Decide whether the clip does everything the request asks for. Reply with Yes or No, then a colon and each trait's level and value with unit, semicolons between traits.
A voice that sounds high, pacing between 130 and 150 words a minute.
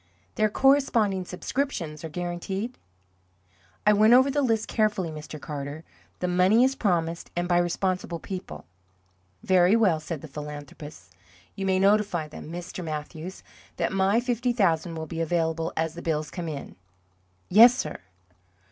No: medium, 180 Hz; average, 145 wpm